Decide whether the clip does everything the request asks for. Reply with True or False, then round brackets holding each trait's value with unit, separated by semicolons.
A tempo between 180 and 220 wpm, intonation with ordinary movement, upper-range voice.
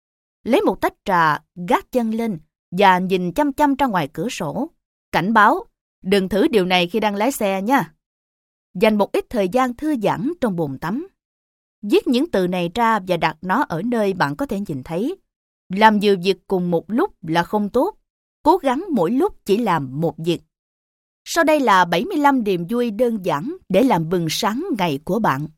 False (195 wpm; 6.7 semitones; 205 Hz)